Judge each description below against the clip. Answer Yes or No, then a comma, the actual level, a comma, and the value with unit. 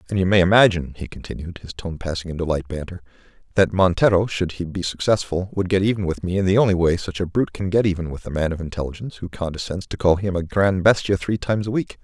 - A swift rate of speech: Yes, fast, 250 wpm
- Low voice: Yes, very low, 90 Hz